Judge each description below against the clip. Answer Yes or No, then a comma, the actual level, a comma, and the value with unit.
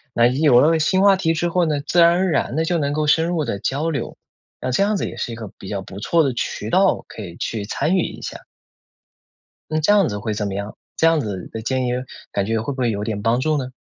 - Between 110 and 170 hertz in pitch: Yes, medium, 140 Hz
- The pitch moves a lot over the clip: Yes, wide, 6.8 semitones